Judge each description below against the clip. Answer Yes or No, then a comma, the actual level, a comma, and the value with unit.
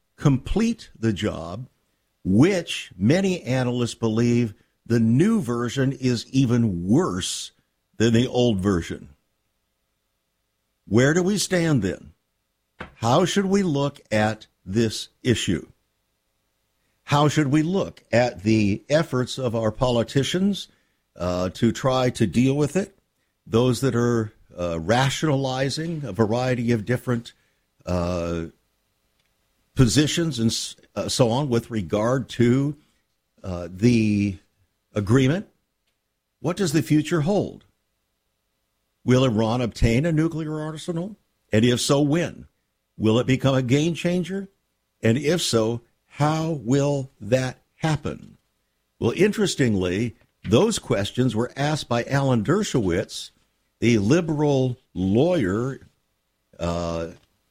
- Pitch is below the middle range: Yes, low, 125 Hz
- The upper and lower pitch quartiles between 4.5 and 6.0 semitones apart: Yes, average, 5.1 semitones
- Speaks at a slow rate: Yes, slow, 110 wpm